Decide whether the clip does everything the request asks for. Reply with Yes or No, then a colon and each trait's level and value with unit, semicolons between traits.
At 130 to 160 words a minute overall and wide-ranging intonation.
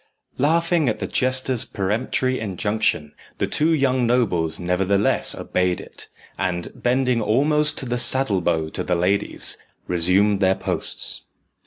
Yes: slow, 135 wpm; wide, 6.0 semitones